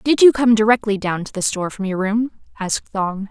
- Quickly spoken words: Yes, fast, 235 wpm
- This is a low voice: No, high, 210 Hz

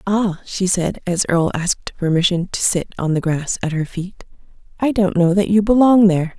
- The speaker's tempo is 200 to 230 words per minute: Yes, fast, 205 wpm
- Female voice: Yes, female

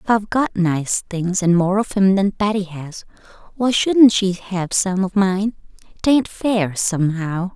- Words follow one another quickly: No, average, 175 wpm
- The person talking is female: Yes, female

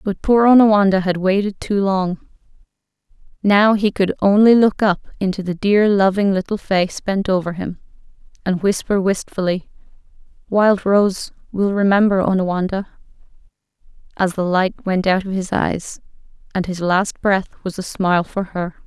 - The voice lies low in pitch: No, high, 195 Hz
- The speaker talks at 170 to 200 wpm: No, average, 150 wpm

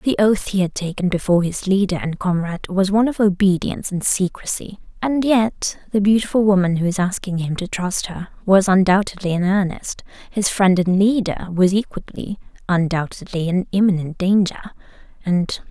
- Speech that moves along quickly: No, average, 165 wpm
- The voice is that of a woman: Yes, female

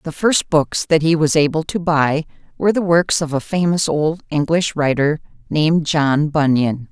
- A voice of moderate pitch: Yes, medium, 155 Hz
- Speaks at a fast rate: No, average, 180 wpm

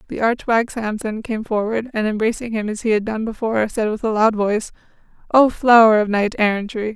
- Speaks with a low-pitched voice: No, high, 220 Hz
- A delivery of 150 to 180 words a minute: No, fast, 205 wpm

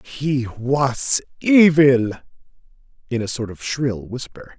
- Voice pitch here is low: Yes, low, 130 Hz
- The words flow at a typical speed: No, slow, 120 wpm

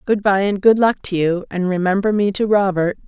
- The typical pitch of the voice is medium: No, high, 195 Hz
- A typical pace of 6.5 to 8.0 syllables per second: No, 5.3 syllables/s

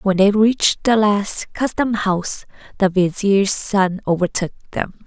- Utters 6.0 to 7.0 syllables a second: No, 4.2 syllables/s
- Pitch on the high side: Yes, high, 200 Hz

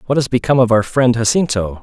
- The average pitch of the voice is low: Yes, low, 120 Hz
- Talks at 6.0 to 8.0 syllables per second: Yes, 6.6 syllables/s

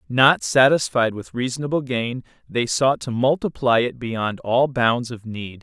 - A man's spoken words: Yes, male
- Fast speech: No, average, 160 wpm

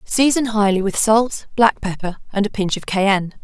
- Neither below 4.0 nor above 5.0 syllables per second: Yes, 4.9 syllables/s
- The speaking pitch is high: Yes, high, 210 Hz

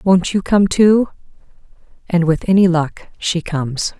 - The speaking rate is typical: Yes, average, 150 wpm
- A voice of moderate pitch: Yes, medium, 180 Hz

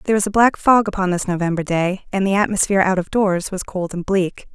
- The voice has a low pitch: No, high, 190 Hz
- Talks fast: Yes, fast, 250 wpm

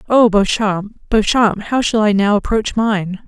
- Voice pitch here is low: No, high, 210 Hz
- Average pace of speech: Yes, average, 165 wpm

